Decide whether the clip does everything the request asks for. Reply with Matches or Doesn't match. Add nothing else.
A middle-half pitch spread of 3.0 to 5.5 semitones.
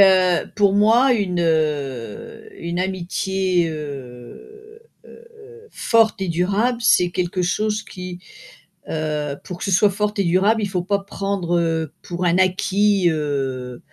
Matches